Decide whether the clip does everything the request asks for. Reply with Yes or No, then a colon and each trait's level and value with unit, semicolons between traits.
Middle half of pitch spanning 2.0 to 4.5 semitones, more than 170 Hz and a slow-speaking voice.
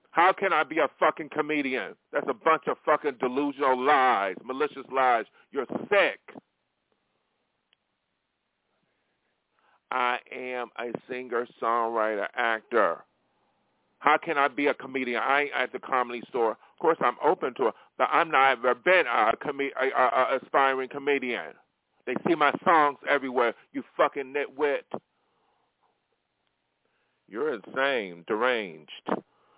No: average, 3.0 semitones; medium, 140 Hz; slow, 130 wpm